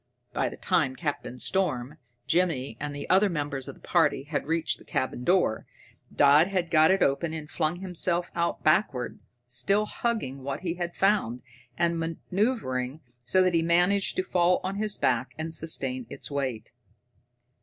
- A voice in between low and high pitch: Yes, medium, 165 Hz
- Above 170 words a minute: No, average, 165 wpm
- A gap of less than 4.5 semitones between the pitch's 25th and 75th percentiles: No, average, 5.0 semitones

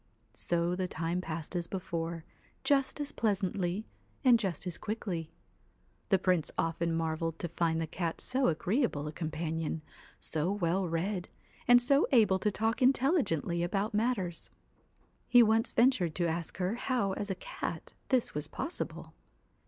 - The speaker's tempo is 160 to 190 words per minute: No, average, 150 wpm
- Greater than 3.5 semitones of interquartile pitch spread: Yes, average, 5.1 semitones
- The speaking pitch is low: No, medium, 180 Hz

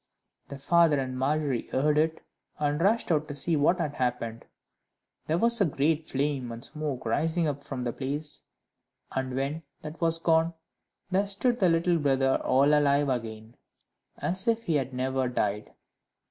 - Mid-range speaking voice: Yes, medium, 145 Hz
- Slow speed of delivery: No, average, 165 wpm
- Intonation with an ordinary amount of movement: Yes, average, 3.7 semitones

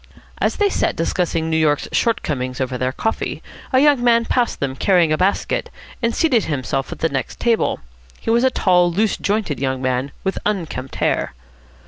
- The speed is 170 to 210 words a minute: Yes, average, 180 wpm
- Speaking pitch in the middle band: Yes, medium, 175 Hz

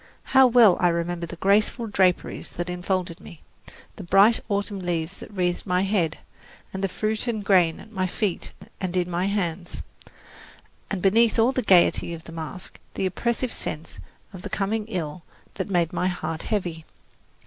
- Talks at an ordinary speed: Yes, average, 170 wpm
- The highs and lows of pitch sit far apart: No, average, 3.1 semitones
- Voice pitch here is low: No, medium, 185 Hz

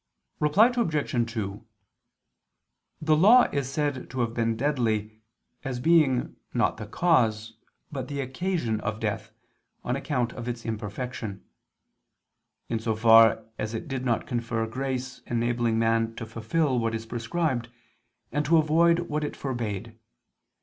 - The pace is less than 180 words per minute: Yes, average, 140 wpm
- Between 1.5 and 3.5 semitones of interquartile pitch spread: No, average, 4.4 semitones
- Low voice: Yes, low, 120 Hz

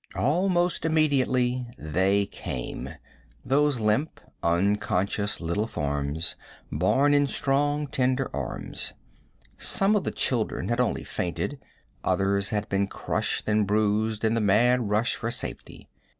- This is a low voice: Yes, low, 110 Hz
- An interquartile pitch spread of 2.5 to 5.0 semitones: No, wide, 5.4 semitones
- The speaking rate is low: Yes, slow, 120 wpm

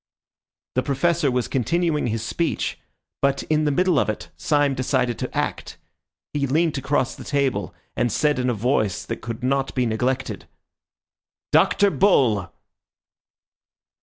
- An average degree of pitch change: Yes, average, 3.2 semitones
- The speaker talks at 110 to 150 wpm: Yes, average, 140 wpm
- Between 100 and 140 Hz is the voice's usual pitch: Yes, low, 135 Hz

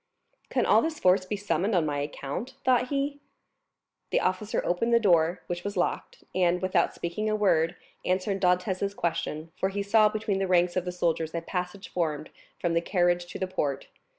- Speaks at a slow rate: No, average, 190 wpm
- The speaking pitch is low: No, medium, 185 Hz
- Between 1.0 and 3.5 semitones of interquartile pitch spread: Yes, average, 2.9 semitones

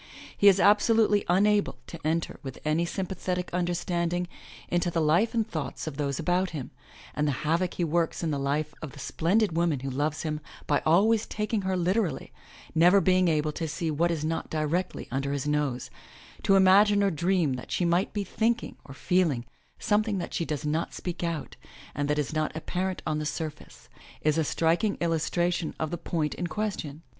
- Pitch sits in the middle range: Yes, medium, 170 Hz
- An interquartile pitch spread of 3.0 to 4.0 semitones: Yes, average, 3.5 semitones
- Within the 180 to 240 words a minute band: Yes, average, 190 wpm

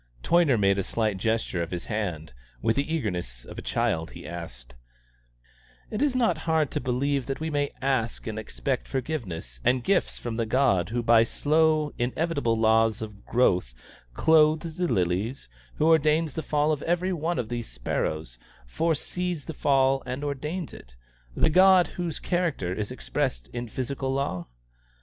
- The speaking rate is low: No, average, 165 wpm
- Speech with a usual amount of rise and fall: No, wide, 7.6 semitones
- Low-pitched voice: Yes, low, 130 Hz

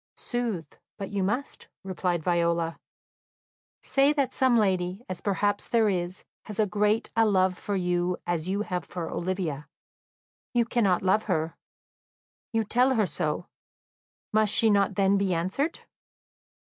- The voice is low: No, high, 195 Hz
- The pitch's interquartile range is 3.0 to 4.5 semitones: Yes, average, 3.4 semitones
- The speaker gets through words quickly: No, average, 145 wpm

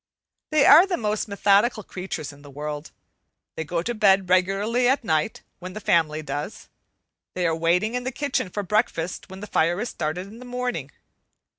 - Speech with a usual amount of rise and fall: No, wide, 5.9 semitones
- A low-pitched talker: No, high, 190 Hz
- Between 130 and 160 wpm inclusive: No, average, 185 wpm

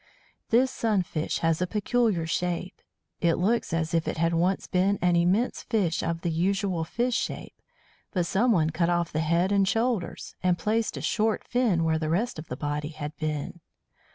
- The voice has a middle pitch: Yes, medium, 175 Hz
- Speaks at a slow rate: No, average, 180 wpm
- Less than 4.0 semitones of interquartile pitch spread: No, average, 4.4 semitones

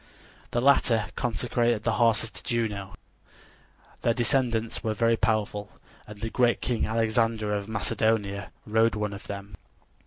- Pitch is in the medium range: No, low, 110 Hz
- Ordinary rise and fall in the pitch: No, narrow, 1.9 semitones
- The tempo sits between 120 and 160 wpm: Yes, slow, 135 wpm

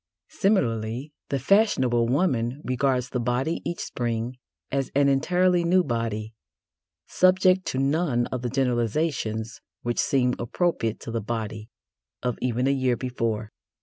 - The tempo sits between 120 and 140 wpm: Yes, slow, 135 wpm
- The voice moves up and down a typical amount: Yes, average, 4.3 semitones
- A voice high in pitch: No, low, 125 Hz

